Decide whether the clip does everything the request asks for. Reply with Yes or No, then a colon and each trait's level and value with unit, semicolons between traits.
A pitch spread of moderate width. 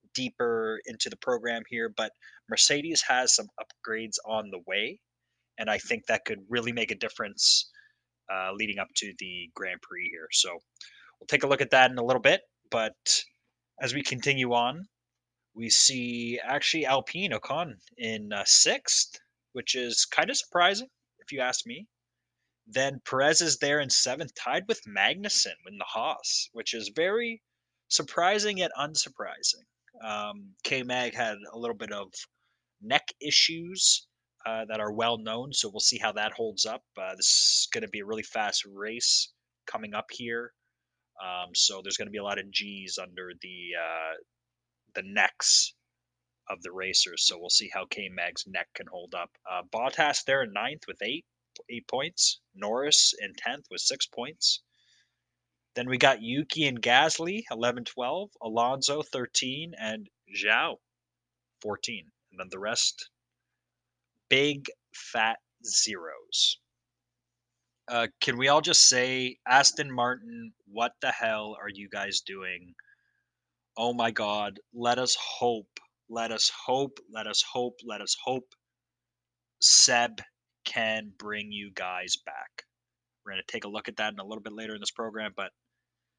Yes: average, 4.0 semitones